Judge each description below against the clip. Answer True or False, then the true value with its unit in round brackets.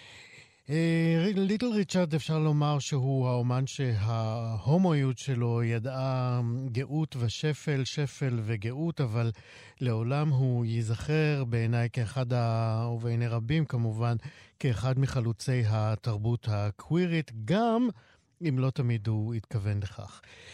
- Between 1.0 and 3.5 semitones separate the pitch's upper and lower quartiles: False (4.3 semitones)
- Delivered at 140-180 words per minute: False (100 wpm)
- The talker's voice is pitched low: True (125 Hz)